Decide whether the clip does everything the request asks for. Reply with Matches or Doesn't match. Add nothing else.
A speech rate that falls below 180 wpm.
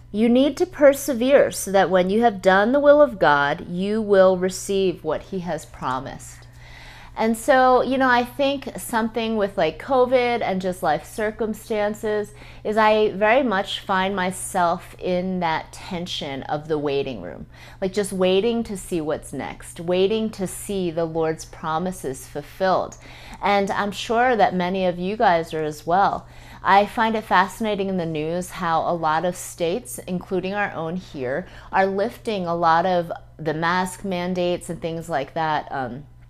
Matches